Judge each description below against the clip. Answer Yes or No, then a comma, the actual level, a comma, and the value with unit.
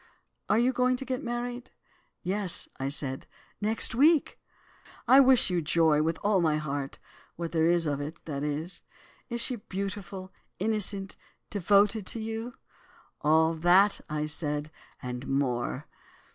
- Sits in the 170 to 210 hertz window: Yes, medium, 185 Hz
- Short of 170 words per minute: Yes, average, 145 wpm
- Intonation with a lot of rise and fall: Yes, wide, 6.5 semitones